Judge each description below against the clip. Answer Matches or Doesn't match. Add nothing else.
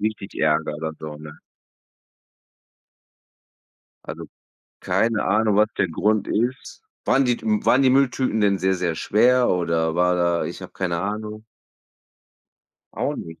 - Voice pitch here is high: Doesn't match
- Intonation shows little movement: Doesn't match